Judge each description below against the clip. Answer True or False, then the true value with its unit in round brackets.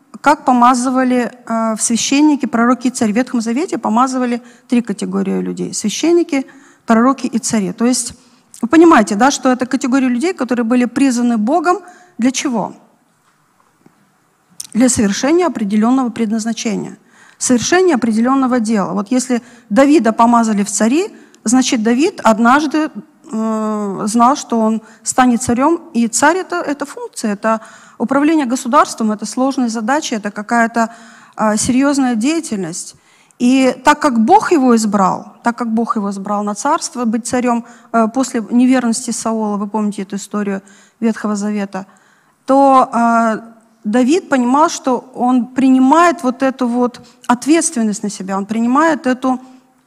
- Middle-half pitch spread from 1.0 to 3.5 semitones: True (3.2 semitones)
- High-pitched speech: True (245 Hz)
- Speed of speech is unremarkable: True (130 wpm)